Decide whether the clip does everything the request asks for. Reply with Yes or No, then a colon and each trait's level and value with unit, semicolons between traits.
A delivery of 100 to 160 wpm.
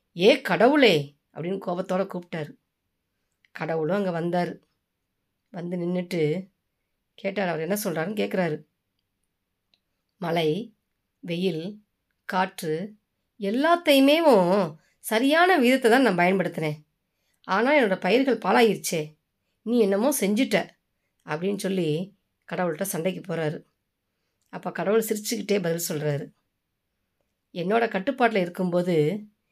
No: average, 90 wpm